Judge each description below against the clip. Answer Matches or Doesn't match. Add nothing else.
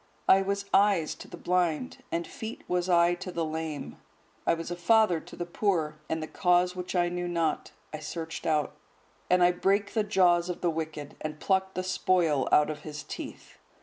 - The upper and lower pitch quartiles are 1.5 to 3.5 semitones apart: Matches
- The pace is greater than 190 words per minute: Matches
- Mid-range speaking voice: Matches